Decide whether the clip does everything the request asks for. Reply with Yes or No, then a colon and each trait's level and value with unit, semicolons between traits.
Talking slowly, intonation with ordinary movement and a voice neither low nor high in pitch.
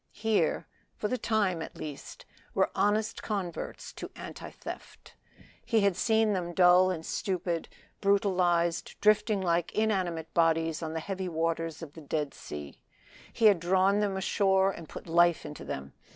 No: average, 155 wpm; average, 3.4 semitones; medium, 180 Hz